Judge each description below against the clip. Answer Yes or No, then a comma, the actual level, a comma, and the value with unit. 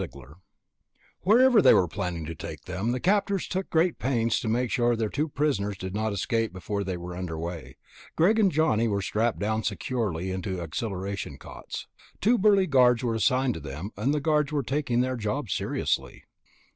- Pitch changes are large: Yes, wide, 7.5 semitones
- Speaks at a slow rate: No, average, 185 wpm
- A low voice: Yes, low, 115 Hz